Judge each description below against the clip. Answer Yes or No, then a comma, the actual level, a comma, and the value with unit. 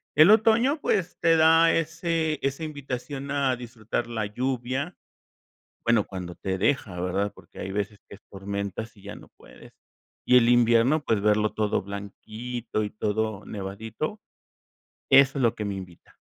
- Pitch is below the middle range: Yes, low, 115 Hz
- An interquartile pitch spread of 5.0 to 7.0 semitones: Yes, wide, 5.5 semitones